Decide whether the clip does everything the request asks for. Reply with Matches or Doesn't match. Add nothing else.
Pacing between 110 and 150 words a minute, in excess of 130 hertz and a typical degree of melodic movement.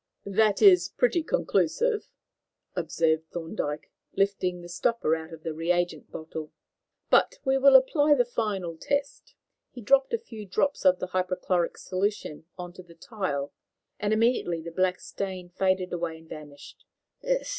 Doesn't match